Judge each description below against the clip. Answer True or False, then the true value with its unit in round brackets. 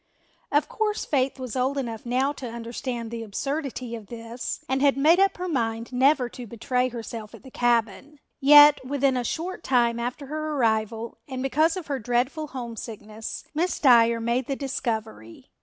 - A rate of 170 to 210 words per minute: True (175 wpm)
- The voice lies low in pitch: False (255 Hz)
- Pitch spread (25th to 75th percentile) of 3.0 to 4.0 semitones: True (3.4 semitones)